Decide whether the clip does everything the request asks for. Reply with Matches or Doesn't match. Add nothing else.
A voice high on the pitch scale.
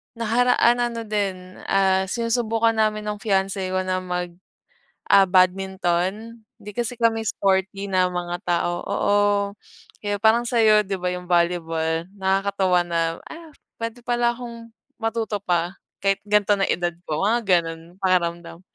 Matches